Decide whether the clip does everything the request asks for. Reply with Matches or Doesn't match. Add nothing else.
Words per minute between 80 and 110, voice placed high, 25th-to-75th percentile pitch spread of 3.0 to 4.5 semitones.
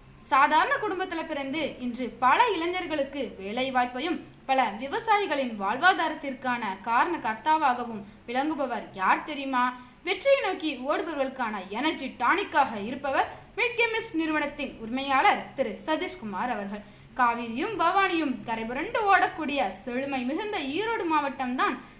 Doesn't match